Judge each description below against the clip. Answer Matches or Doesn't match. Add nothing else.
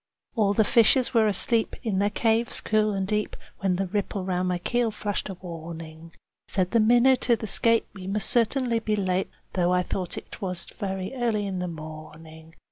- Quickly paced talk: Doesn't match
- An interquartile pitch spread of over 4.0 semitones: Doesn't match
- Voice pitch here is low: Doesn't match